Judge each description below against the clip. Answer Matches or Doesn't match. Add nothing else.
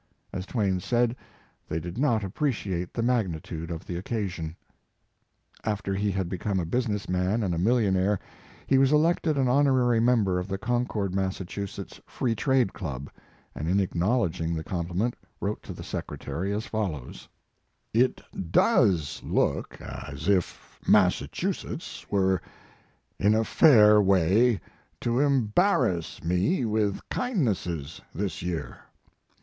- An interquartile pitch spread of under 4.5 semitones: Doesn't match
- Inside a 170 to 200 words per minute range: Doesn't match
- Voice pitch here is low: Matches